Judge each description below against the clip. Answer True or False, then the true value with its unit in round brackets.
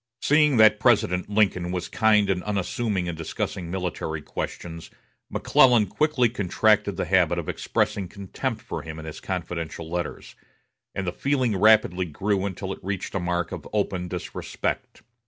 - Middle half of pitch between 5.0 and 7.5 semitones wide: False (3.4 semitones)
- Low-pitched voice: True (95 Hz)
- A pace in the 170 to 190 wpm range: False (155 wpm)